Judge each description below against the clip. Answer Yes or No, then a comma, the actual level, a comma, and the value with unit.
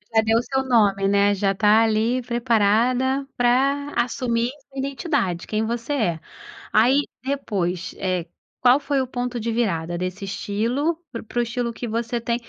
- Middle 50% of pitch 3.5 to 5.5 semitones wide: Yes, average, 3.8 semitones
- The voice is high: Yes, high, 235 Hz